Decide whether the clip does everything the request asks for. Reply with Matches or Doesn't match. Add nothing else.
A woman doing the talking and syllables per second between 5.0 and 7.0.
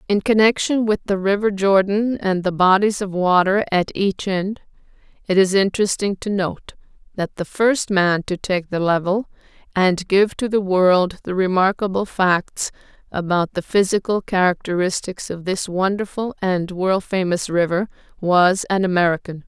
Doesn't match